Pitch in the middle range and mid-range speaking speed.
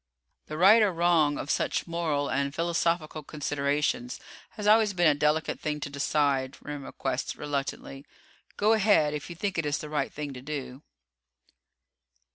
Yes: medium, 150 Hz; average, 160 wpm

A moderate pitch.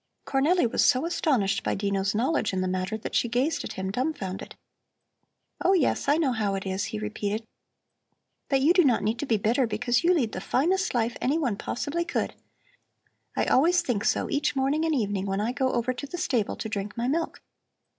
No: high, 245 Hz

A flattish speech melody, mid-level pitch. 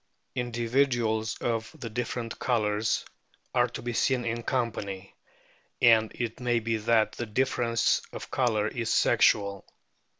No: narrow, 1.8 semitones; low, 115 Hz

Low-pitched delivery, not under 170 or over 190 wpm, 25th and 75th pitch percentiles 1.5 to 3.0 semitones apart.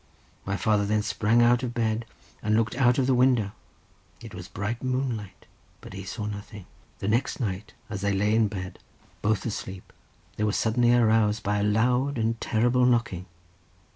Yes: low, 110 Hz; average, 175 wpm; average, 2.7 semitones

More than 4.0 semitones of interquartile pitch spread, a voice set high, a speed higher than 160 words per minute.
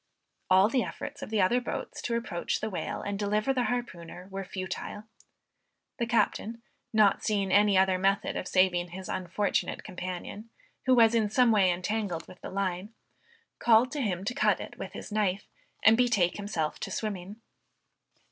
No: average, 3.3 semitones; high, 205 Hz; average, 170 wpm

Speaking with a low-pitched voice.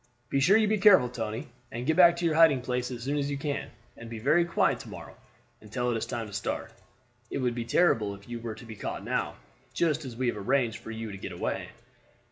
Yes: low, 125 Hz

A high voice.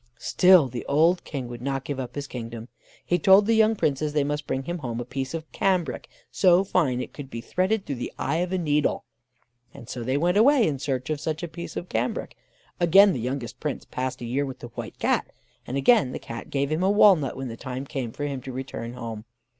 No: medium, 140 Hz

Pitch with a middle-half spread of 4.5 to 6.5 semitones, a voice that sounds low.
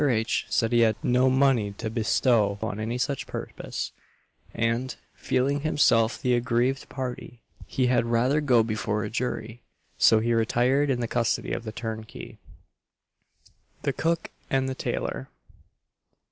No: narrow, 2.6 semitones; low, 120 Hz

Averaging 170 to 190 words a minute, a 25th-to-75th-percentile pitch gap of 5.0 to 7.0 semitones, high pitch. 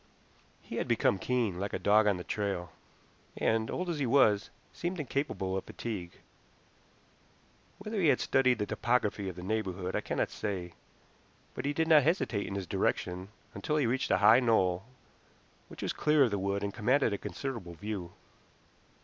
No: average, 175 wpm; wide, 5.6 semitones; low, 110 Hz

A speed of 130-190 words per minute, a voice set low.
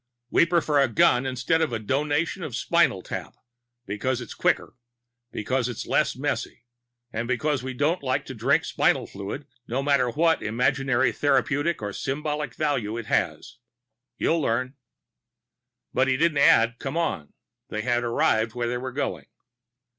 Yes: average, 160 wpm; low, 130 Hz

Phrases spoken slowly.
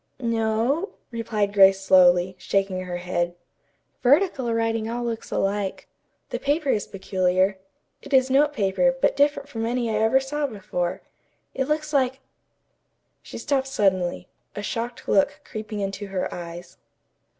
No: average, 145 wpm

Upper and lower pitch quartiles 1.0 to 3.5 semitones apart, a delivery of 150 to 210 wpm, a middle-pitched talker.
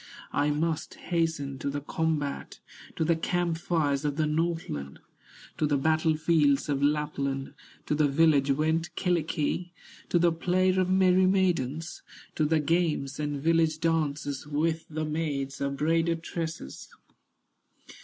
No: narrow, 2.4 semitones; average, 140 wpm; medium, 155 Hz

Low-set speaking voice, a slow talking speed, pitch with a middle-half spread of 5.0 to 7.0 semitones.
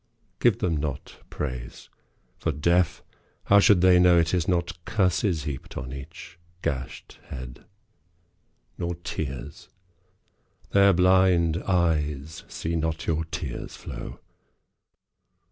No: very low, 85 Hz; slow, 110 wpm; average, 3.5 semitones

